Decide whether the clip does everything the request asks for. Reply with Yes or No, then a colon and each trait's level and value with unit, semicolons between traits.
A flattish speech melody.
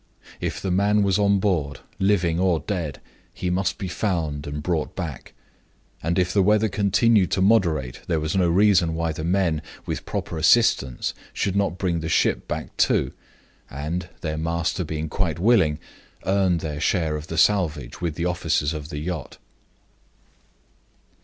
No: average, 3.7 semitones